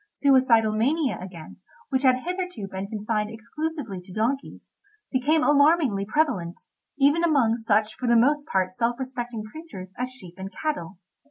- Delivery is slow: No, average, 150 wpm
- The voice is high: Yes, high, 240 Hz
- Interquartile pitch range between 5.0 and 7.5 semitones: Yes, average, 5.3 semitones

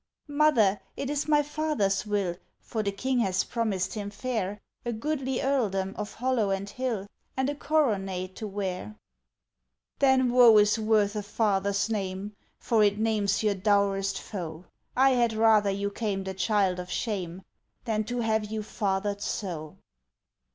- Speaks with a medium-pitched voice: No, high, 210 Hz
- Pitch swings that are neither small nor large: Yes, average, 3.3 semitones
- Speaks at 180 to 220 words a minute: No, average, 155 wpm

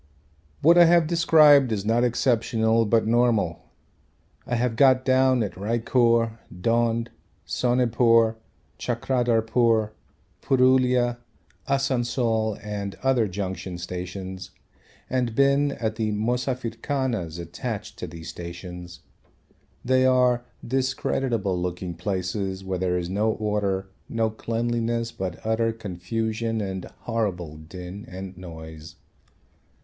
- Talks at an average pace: No, slow, 105 wpm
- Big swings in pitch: No, average, 4.5 semitones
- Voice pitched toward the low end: Yes, low, 115 Hz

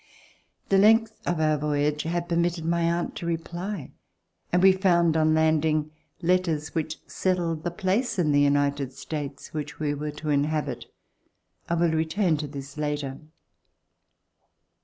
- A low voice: No, medium, 160 Hz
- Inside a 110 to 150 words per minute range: Yes, average, 145 wpm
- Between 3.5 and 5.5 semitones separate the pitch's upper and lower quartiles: No, average, 2.7 semitones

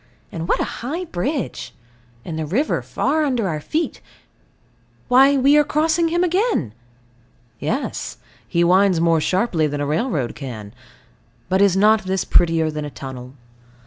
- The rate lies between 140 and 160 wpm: Yes, average, 150 wpm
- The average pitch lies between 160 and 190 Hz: Yes, medium, 185 Hz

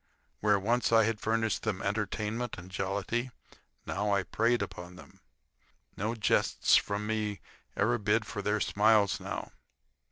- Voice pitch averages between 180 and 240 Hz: No, low, 105 Hz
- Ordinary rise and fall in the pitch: No, narrow, 2.0 semitones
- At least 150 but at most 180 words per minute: No, average, 140 wpm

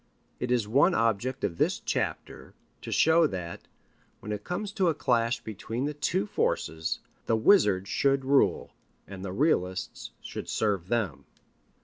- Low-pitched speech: Yes, low, 115 Hz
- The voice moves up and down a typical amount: No, wide, 6.0 semitones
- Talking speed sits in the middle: Yes, average, 150 wpm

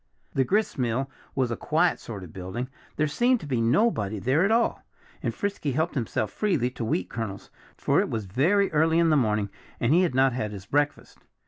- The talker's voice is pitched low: Yes, low, 130 Hz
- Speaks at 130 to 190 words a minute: No, fast, 205 wpm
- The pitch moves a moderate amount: No, wide, 6.6 semitones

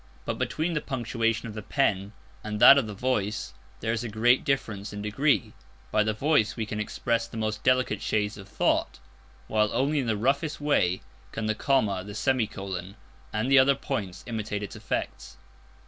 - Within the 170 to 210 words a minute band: Yes, average, 185 wpm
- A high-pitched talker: No, low, 110 Hz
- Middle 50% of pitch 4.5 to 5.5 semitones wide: No, average, 3.9 semitones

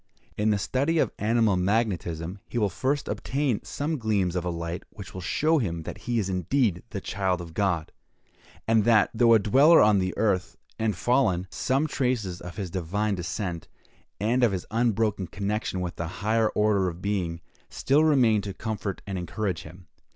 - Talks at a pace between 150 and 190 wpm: Yes, average, 180 wpm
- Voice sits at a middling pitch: No, low, 105 Hz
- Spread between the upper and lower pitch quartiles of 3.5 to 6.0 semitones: Yes, average, 4.1 semitones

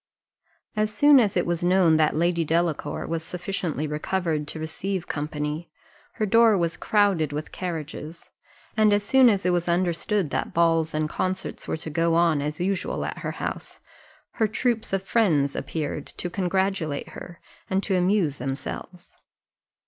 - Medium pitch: Yes, medium, 175 Hz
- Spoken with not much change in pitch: No, average, 3.6 semitones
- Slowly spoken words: No, average, 160 wpm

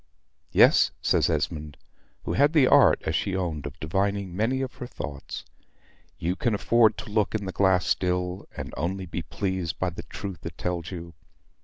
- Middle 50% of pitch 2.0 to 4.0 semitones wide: Yes, average, 3.2 semitones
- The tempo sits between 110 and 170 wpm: No, average, 180 wpm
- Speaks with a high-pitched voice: No, very low, 95 Hz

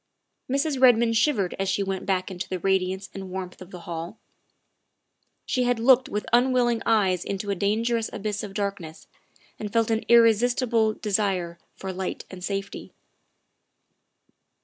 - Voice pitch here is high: Yes, high, 205 Hz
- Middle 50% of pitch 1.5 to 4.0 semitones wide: Yes, average, 3.4 semitones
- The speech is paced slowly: No, average, 150 wpm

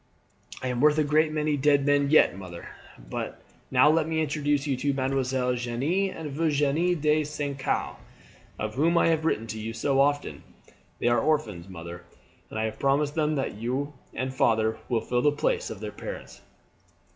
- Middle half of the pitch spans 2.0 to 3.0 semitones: No, average, 3.8 semitones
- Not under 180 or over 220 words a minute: Yes, average, 185 wpm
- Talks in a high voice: No, medium, 140 Hz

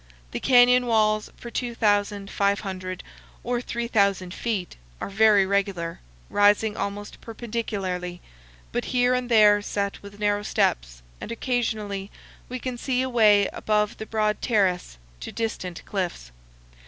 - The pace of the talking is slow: Yes, slow, 125 wpm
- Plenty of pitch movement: No, average, 2.8 semitones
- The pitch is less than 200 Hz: No, high, 205 Hz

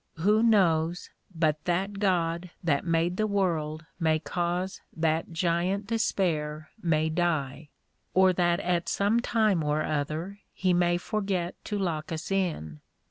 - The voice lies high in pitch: No, medium, 175 Hz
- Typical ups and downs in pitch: Yes, average, 3.3 semitones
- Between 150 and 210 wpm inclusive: No, slow, 135 wpm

